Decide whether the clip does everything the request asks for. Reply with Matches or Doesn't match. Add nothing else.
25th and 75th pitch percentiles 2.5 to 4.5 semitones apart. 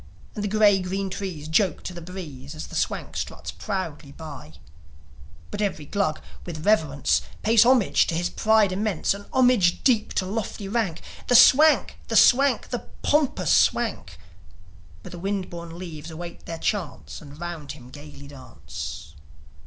Doesn't match